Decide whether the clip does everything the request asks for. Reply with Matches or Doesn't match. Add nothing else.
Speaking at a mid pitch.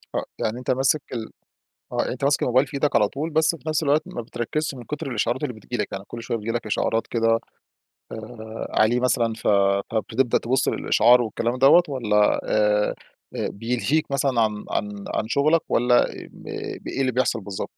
Doesn't match